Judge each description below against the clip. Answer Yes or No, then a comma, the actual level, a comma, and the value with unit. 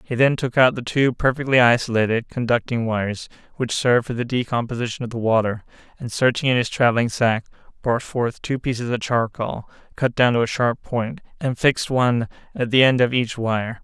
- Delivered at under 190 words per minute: No, average, 195 wpm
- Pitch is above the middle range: No, low, 120 Hz